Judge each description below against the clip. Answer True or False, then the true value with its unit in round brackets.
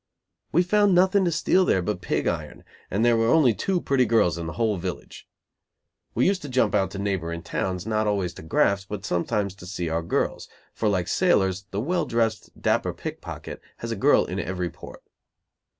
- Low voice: True (105 Hz)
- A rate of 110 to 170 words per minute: False (195 wpm)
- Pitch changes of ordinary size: False (6.2 semitones)